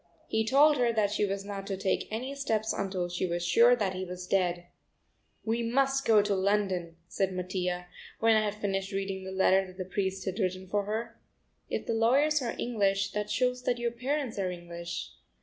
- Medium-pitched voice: No, high, 200 Hz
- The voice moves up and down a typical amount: Yes, average, 3.6 semitones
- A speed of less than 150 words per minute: No, average, 200 wpm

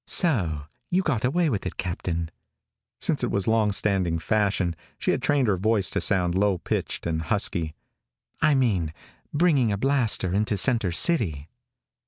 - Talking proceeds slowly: No, average, 160 wpm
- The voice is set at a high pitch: No, low, 100 Hz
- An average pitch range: No, wide, 6.4 semitones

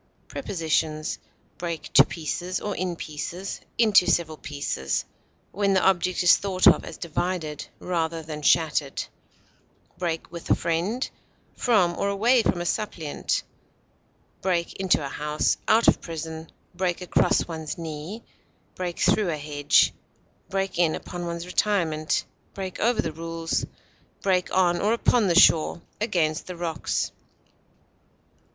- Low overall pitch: No, medium, 175 Hz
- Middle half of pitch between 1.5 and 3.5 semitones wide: Yes, average, 3.0 semitones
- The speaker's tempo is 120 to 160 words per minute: Yes, slow, 135 wpm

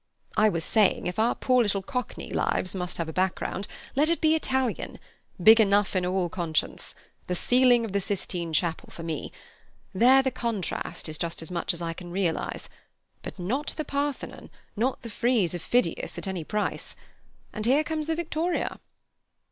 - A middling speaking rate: Yes, average, 180 wpm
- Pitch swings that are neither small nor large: No, wide, 6.3 semitones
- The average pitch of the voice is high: Yes, high, 205 Hz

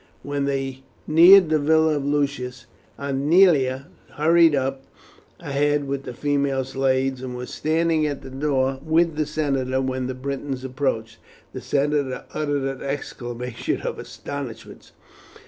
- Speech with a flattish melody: Yes, narrow, 2.2 semitones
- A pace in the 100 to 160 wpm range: Yes, slow, 135 wpm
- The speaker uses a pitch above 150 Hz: No, medium, 140 Hz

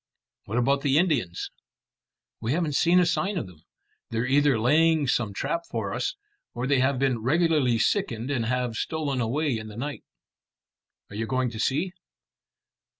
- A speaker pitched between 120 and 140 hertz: Yes, low, 135 Hz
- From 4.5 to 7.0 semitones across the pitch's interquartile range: Yes, average, 4.9 semitones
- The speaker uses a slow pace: No, average, 165 wpm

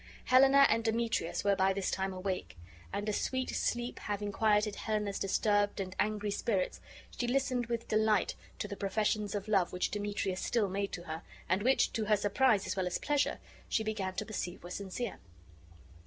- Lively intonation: No, narrow, 2.5 semitones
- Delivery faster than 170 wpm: Yes, average, 185 wpm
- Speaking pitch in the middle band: No, high, 205 Hz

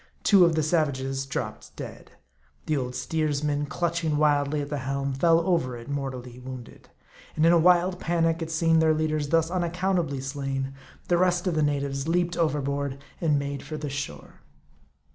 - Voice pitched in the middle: Yes, medium, 150 Hz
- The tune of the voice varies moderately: Yes, average, 3.3 semitones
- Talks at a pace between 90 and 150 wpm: No, average, 170 wpm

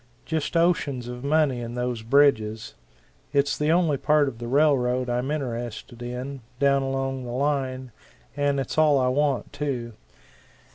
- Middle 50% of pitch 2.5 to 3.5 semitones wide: Yes, average, 2.8 semitones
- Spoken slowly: No, average, 150 wpm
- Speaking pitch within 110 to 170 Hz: Yes, low, 135 Hz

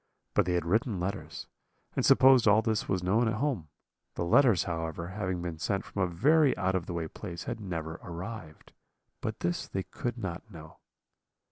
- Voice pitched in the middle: No, very low, 95 Hz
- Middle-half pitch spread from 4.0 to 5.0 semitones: Yes, average, 4.5 semitones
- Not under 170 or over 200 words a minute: Yes, average, 190 wpm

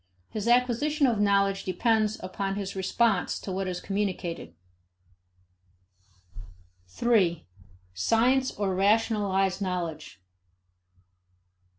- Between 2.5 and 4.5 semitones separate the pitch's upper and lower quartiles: Yes, average, 3.4 semitones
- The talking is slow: Yes, slow, 85 wpm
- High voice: Yes, high, 200 Hz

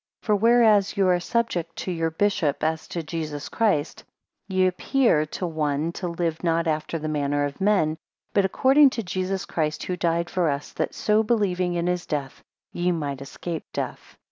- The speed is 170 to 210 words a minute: Yes, average, 185 wpm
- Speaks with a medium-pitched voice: Yes, medium, 175 Hz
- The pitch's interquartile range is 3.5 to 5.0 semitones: Yes, average, 3.8 semitones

